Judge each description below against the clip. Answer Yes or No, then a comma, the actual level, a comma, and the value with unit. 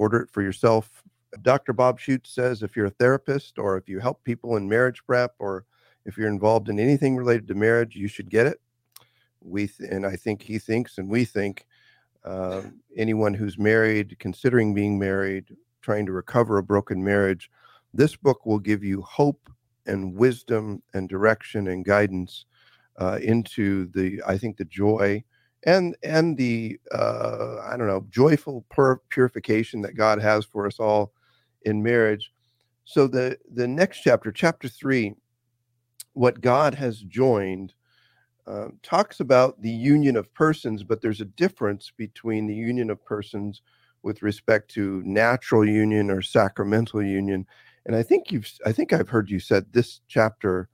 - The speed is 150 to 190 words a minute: Yes, average, 165 wpm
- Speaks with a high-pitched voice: No, low, 110 Hz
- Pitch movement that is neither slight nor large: Yes, average, 3.3 semitones